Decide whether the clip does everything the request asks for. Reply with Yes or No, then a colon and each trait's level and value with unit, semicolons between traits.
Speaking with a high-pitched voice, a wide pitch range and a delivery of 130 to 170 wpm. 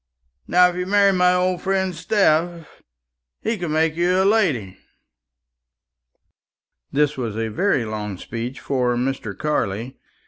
No: medium, 160 Hz; wide, 7.0 semitones; slow, 135 wpm